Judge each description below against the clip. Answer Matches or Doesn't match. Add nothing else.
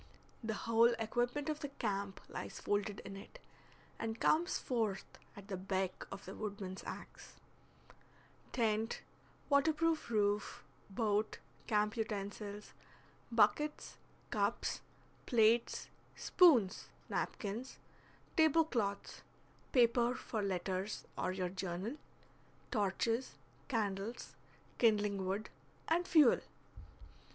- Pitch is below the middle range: Doesn't match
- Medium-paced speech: Doesn't match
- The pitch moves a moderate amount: Matches